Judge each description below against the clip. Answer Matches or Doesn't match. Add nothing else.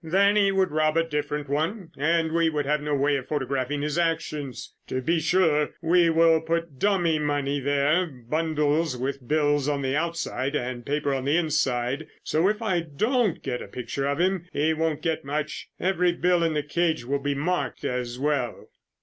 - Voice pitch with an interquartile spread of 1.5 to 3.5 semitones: Matches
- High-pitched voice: Doesn't match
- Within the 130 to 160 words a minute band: Doesn't match